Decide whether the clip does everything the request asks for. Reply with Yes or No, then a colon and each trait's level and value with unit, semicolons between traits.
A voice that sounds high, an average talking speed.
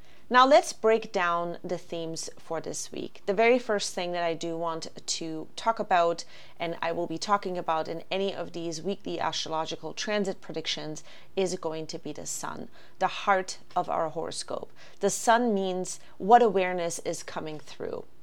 No: medium, 180 Hz; average, 175 wpm